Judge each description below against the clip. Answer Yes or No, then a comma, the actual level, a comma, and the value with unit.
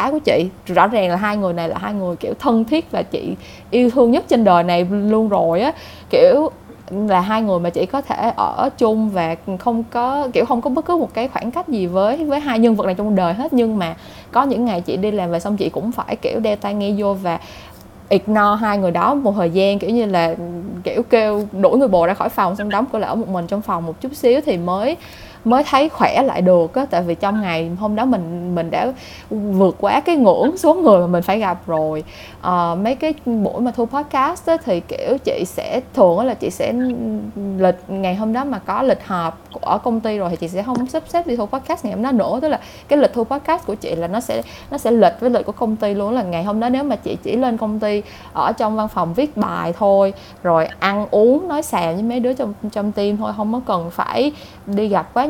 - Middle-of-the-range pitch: No, high, 215 Hz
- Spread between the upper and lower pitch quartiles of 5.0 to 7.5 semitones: Yes, wide, 5.4 semitones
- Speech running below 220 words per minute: No, fast, 250 wpm